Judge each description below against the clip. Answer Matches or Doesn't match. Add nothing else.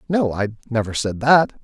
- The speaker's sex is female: Doesn't match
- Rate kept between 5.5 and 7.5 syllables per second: Doesn't match